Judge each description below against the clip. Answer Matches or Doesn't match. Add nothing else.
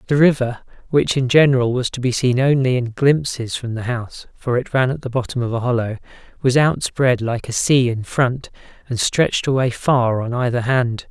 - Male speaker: Matches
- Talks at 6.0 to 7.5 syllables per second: Doesn't match